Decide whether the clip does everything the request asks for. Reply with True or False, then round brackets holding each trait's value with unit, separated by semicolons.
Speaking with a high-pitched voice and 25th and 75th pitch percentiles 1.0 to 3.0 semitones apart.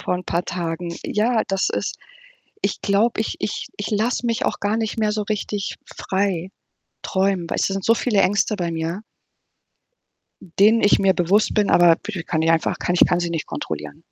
False (195 Hz; 3.5 semitones)